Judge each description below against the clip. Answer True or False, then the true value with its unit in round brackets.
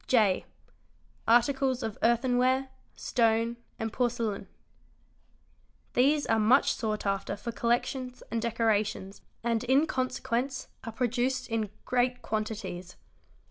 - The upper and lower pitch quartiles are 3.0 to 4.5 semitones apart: False (2.6 semitones)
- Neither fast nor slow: False (105 wpm)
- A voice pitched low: False (235 Hz)